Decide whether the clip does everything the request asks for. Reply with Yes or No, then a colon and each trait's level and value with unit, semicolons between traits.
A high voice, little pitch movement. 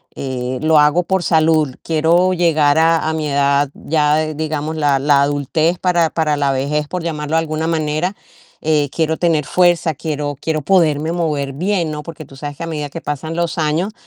No: medium, 155 Hz; narrow, 2.1 semitones